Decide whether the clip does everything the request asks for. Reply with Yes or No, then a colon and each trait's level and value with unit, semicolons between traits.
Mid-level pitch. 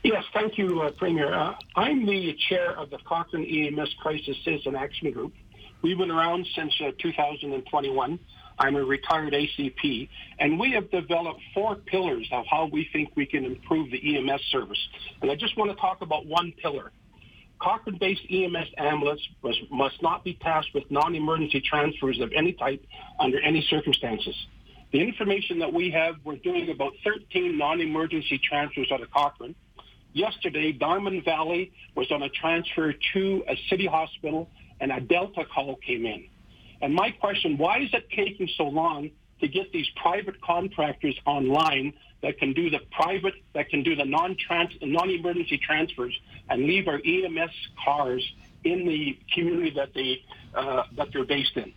Yes: medium, 160 Hz